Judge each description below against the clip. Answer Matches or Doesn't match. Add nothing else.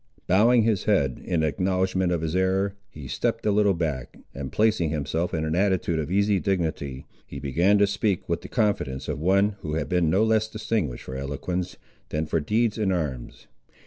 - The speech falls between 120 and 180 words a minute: Doesn't match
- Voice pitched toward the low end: Matches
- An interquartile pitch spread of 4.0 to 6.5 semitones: Matches